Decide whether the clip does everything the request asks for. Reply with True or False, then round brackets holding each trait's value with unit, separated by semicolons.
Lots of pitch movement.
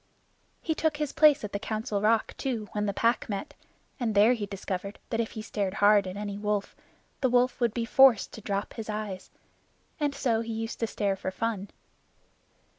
False (2.7 semitones)